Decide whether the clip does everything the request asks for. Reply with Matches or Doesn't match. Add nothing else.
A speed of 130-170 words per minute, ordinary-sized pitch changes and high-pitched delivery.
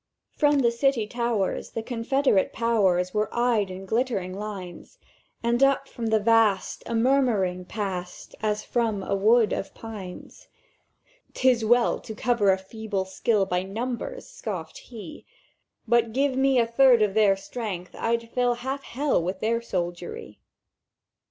Matches